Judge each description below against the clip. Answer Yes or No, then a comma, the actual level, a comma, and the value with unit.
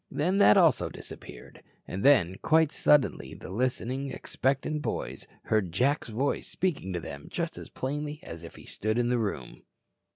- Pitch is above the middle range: No, low, 130 Hz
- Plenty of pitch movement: Yes, wide, 7.0 semitones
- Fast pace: No, average, 165 wpm